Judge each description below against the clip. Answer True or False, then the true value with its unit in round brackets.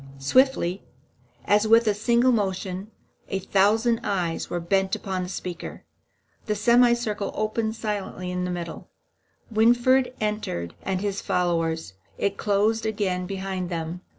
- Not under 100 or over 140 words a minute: True (135 wpm)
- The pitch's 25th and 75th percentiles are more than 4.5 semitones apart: False (3.4 semitones)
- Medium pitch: False (200 Hz)